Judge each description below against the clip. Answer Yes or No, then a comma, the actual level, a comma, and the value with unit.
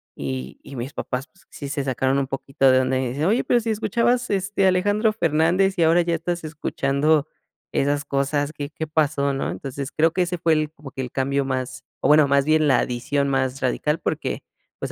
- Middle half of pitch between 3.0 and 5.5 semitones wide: Yes, average, 3.6 semitones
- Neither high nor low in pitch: Yes, medium, 145 Hz